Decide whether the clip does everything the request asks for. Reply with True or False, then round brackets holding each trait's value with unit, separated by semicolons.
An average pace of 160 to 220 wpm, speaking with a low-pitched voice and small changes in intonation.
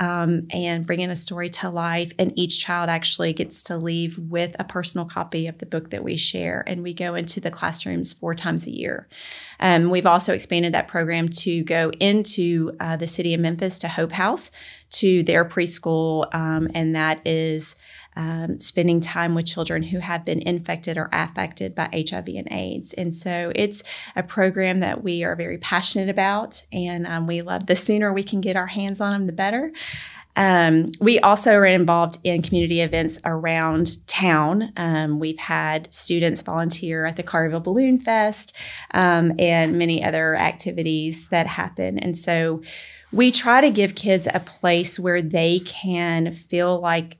False (180 wpm; 170 Hz; 2.0 semitones)